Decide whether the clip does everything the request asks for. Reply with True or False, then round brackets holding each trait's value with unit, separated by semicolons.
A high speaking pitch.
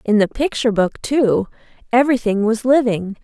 True (230 Hz)